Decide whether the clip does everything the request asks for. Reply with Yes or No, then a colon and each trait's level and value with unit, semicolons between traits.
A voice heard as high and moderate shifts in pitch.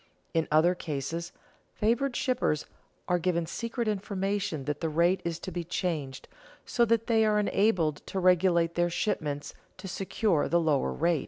No: medium, 175 Hz; average, 4.3 semitones